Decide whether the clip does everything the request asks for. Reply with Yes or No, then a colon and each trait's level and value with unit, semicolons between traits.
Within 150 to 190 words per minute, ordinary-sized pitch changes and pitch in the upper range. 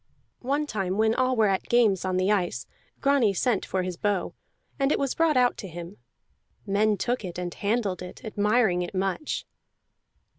Yes: average, 180 wpm; average, 4.7 semitones; high, 205 Hz